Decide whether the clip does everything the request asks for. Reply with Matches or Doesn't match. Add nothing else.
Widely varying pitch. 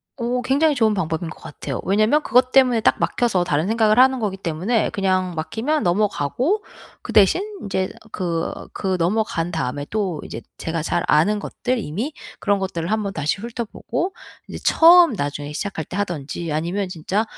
Matches